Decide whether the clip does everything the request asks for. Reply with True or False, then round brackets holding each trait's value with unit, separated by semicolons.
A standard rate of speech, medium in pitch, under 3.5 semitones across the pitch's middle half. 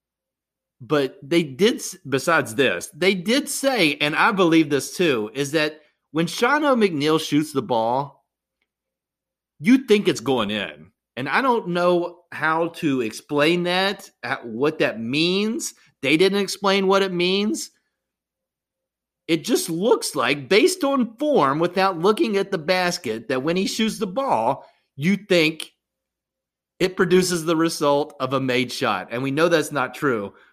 False (150 wpm; 175 Hz; 5.0 semitones)